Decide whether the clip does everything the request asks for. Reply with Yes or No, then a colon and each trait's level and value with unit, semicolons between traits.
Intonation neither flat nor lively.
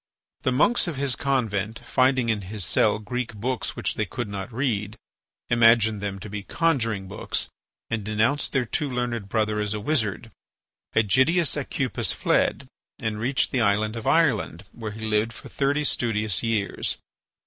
Yes: average, 3.4 semitones